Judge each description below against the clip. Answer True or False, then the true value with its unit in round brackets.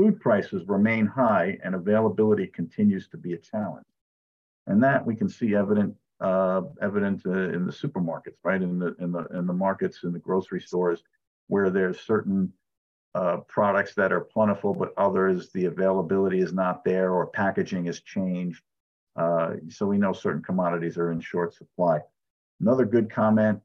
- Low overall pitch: True (95 Hz)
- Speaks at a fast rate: False (170 wpm)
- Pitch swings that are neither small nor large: True (3.0 semitones)